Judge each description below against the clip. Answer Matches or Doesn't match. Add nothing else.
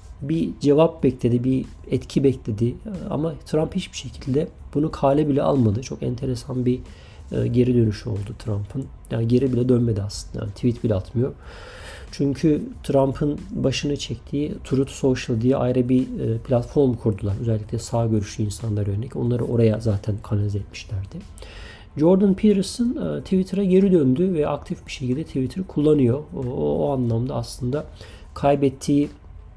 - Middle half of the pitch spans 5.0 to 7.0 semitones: Doesn't match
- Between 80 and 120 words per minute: Doesn't match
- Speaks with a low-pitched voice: Matches